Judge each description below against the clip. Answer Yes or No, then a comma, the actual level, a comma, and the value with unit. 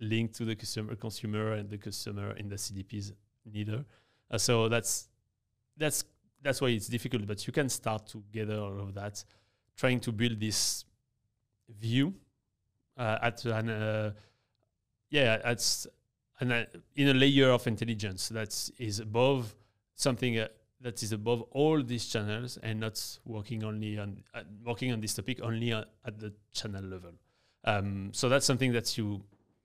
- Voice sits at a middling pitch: No, low, 110 Hz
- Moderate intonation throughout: No, narrow, 2.2 semitones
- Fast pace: No, average, 160 wpm